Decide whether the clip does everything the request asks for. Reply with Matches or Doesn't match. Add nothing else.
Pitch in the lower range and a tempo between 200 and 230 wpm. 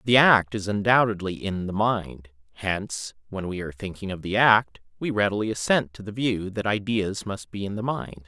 Matches